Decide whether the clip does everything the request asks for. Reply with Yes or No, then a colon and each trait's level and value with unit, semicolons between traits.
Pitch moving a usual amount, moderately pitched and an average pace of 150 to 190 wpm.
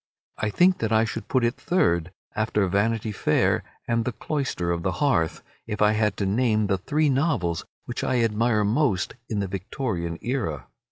No: average, 4.2 semitones; low, 110 Hz; average, 180 wpm